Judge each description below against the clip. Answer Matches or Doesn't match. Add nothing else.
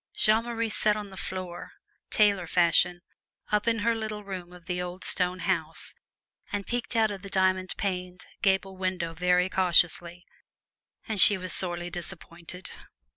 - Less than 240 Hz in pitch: Matches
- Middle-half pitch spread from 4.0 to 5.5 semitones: Doesn't match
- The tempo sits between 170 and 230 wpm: Doesn't match